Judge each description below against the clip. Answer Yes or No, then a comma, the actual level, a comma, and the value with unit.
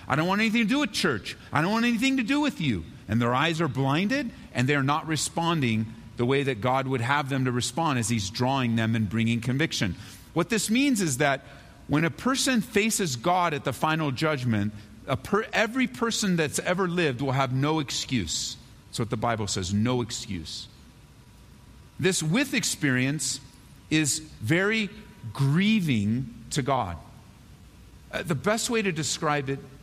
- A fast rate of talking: No, average, 175 wpm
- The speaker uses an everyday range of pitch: No, wide, 6.6 semitones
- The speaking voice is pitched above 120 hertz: Yes, medium, 140 Hz